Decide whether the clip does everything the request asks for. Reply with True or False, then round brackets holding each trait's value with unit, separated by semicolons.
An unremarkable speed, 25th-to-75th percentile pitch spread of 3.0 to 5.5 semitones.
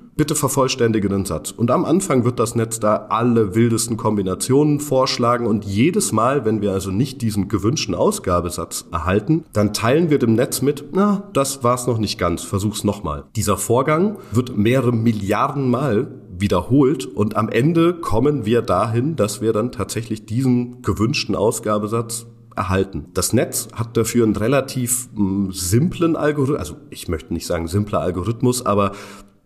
True (160 wpm; 4.3 semitones)